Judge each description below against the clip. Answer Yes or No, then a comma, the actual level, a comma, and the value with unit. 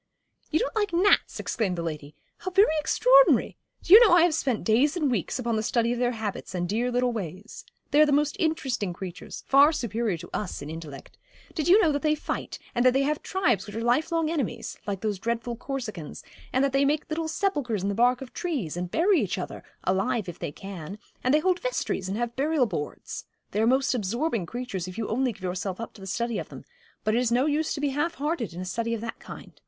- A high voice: Yes, high, 240 Hz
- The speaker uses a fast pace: Yes, fast, 240 wpm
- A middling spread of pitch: No, wide, 7.0 semitones